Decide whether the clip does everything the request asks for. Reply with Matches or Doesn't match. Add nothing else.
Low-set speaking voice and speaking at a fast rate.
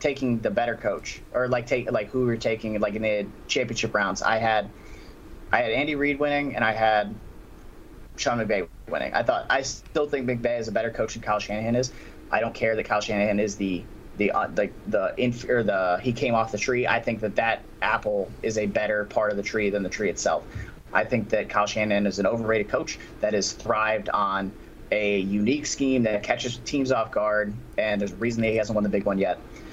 Matches